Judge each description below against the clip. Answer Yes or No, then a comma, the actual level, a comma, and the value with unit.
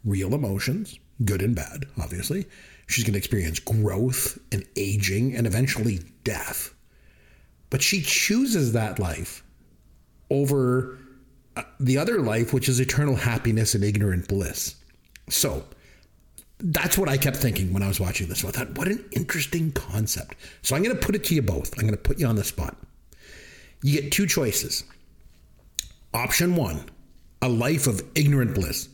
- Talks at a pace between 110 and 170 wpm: Yes, average, 160 wpm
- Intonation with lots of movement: Yes, wide, 6.3 semitones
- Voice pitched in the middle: No, low, 115 Hz